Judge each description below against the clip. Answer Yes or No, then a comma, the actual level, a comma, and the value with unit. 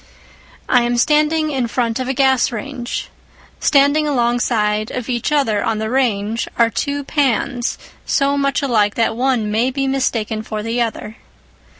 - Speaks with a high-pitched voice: Yes, high, 245 Hz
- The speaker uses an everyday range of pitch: Yes, average, 3.6 semitones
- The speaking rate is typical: Yes, average, 160 wpm